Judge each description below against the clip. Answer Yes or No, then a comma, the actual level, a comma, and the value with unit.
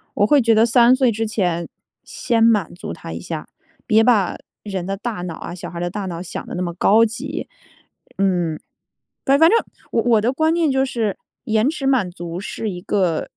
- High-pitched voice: Yes, high, 215 Hz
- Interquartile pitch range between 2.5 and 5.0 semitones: No, wide, 5.4 semitones